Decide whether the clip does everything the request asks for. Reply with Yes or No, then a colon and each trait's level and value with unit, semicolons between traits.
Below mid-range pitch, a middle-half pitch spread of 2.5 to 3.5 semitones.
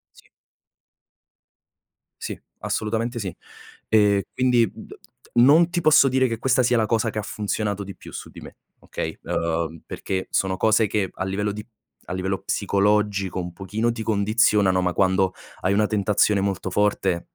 Yes: low, 105 Hz; average, 2.8 semitones